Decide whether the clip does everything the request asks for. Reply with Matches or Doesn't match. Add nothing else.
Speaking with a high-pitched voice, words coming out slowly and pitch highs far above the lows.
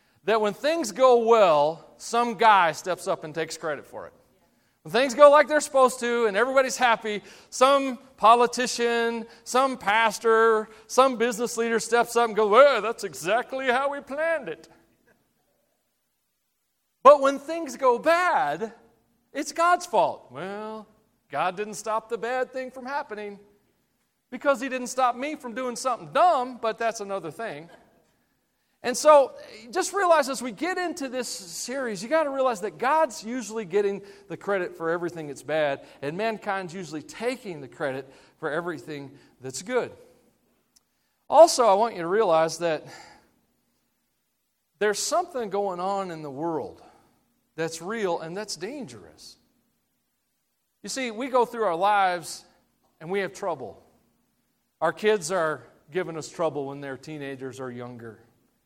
Doesn't match